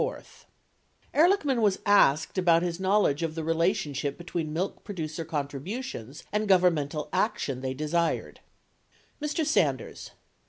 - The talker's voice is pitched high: No, medium, 170 Hz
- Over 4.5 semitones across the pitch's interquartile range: Yes, average, 5.1 semitones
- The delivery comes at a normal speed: No, slow, 120 wpm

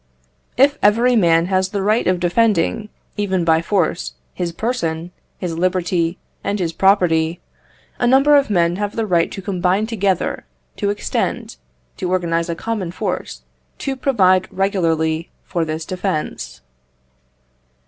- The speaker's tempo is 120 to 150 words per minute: Yes, average, 140 wpm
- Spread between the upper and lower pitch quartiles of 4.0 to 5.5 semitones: No, average, 3.6 semitones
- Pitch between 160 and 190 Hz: Yes, medium, 185 Hz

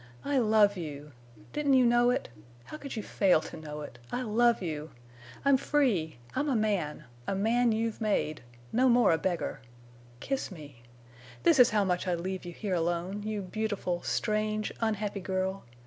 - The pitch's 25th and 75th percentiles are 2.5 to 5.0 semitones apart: No, wide, 5.6 semitones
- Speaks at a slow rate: No, average, 165 wpm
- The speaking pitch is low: No, high, 205 Hz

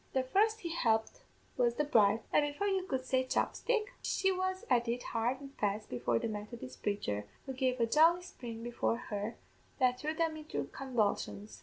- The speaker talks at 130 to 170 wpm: No, average, 185 wpm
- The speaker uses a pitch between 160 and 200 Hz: No, very high, 255 Hz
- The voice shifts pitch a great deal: Yes, wide, 6.0 semitones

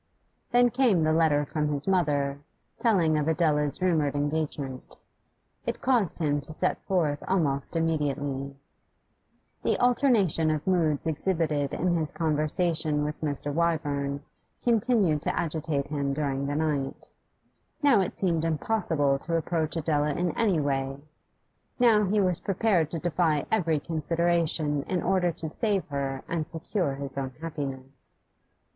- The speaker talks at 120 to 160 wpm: Yes, average, 140 wpm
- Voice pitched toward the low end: No, medium, 155 Hz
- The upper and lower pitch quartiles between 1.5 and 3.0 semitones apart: No, average, 3.4 semitones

